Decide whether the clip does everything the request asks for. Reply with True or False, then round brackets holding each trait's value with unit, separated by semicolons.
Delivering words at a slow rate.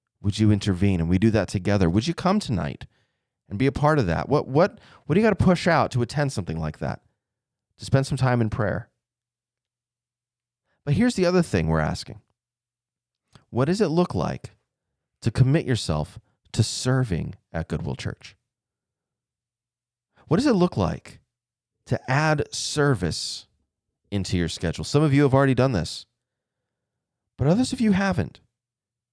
False (165 wpm)